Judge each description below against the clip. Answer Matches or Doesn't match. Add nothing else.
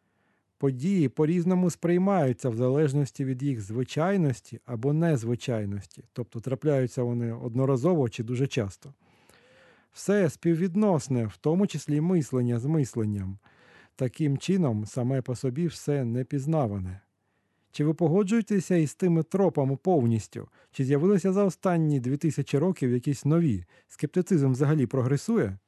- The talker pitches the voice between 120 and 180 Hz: Matches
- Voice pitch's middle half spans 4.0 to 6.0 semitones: Matches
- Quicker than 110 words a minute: Matches